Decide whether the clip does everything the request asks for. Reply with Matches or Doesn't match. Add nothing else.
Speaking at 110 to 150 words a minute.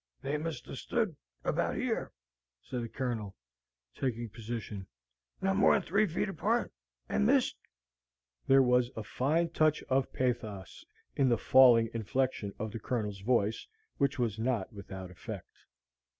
Matches